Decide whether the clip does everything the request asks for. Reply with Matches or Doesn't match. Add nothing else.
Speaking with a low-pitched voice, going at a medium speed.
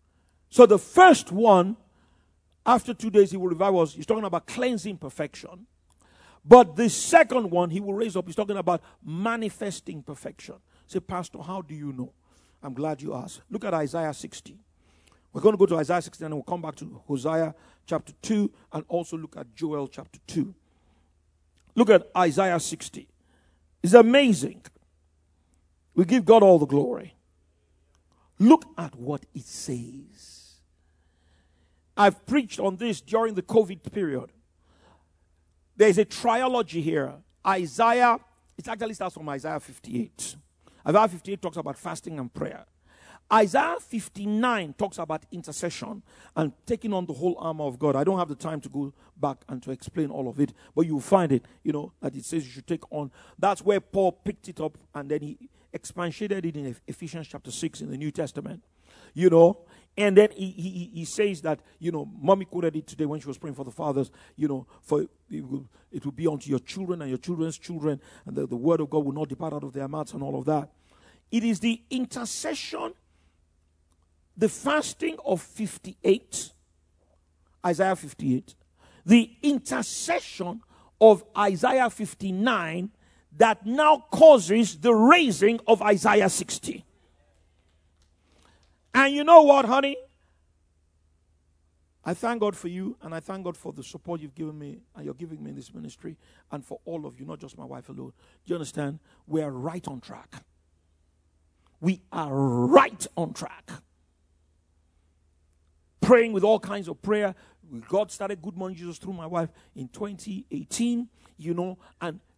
Doesn't match